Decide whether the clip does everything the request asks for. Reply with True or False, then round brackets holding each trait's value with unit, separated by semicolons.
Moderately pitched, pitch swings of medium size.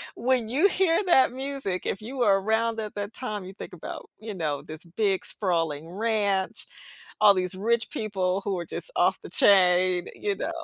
False (205 Hz; 4.0 semitones)